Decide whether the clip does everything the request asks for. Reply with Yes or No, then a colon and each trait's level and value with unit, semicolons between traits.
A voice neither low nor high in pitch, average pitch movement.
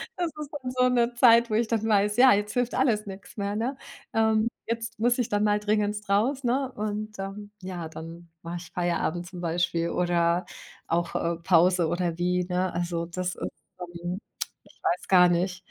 No: high, 200 Hz; average, 4.4 semitones